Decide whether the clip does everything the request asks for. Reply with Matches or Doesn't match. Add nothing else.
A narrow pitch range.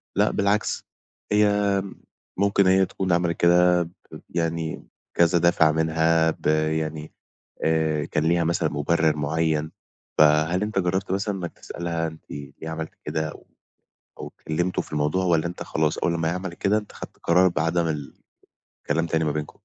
Matches